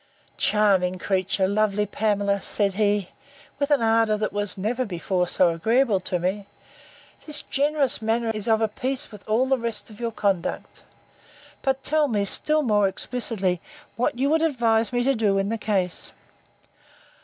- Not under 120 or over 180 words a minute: Yes, average, 160 wpm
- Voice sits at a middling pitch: No, high, 215 Hz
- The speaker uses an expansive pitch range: No, average, 3.5 semitones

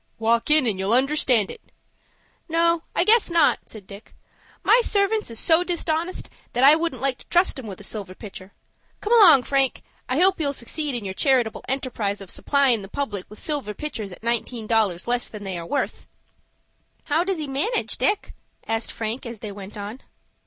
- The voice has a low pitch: No, very high, 250 Hz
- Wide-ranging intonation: Yes, wide, 6.9 semitones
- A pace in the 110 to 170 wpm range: No, average, 190 wpm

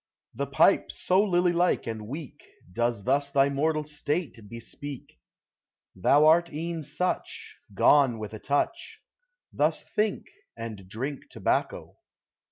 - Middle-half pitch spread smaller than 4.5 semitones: No, wide, 5.6 semitones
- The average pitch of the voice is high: No, medium, 145 Hz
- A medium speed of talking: No, slow, 130 wpm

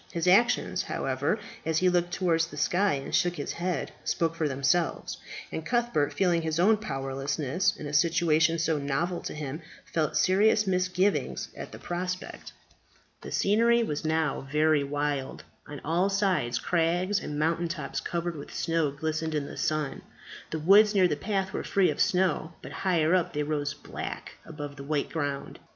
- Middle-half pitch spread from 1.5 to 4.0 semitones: Yes, average, 3.6 semitones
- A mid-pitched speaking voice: Yes, medium, 165 Hz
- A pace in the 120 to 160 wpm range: No, average, 170 wpm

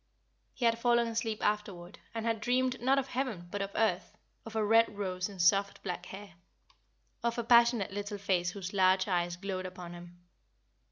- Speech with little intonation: No, average, 3.8 semitones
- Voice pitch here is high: Yes, high, 205 Hz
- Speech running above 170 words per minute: Yes, average, 185 wpm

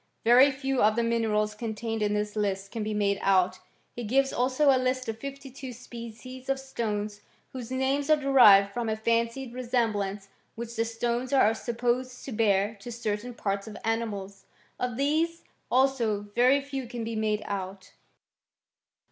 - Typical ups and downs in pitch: Yes, average, 3.5 semitones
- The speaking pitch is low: No, high, 230 Hz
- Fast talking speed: No, average, 165 wpm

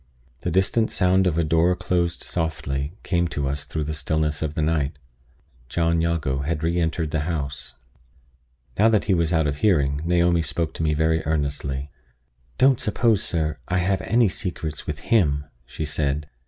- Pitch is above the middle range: No, very low, 80 Hz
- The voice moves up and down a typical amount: Yes, average, 3.1 semitones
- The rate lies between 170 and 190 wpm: Yes, average, 175 wpm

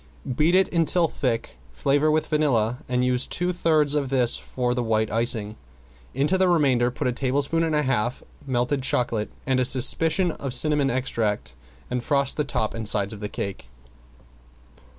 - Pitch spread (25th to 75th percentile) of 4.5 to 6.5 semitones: No, average, 4.1 semitones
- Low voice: Yes, low, 130 Hz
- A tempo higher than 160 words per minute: Yes, average, 170 wpm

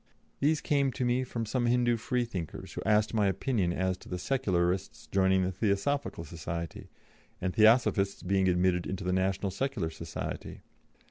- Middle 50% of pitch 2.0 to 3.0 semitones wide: No, average, 5.0 semitones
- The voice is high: No, low, 100 Hz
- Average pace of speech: Yes, average, 150 wpm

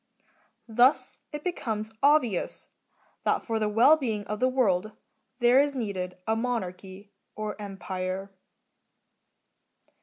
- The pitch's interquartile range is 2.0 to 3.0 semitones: No, average, 4.3 semitones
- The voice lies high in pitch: Yes, high, 215 Hz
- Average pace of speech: No, slow, 115 wpm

